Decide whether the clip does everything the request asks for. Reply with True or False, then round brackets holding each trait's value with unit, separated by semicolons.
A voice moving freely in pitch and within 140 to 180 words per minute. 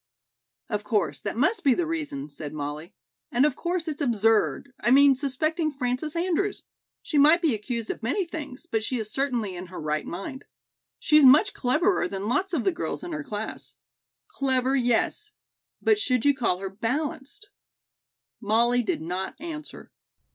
True (6.1 semitones; 170 wpm)